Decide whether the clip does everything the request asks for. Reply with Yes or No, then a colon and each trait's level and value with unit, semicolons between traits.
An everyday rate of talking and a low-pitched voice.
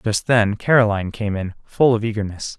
No: fast, 210 wpm; low, 110 Hz